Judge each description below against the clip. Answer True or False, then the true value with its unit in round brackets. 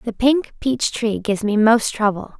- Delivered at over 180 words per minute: True (200 wpm)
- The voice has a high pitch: True (225 Hz)